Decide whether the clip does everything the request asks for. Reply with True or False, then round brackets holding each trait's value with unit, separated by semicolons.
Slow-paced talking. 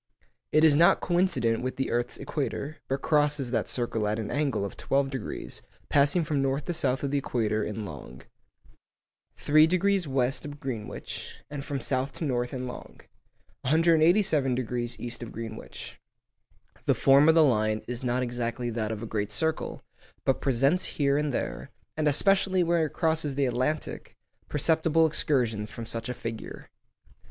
False (165 wpm)